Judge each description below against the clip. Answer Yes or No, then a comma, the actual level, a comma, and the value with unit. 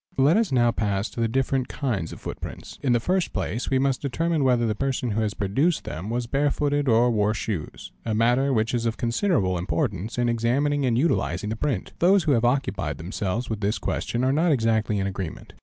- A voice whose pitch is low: Yes, low, 120 Hz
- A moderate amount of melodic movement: Yes, average, 4.4 semitones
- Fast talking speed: Yes, fast, 215 wpm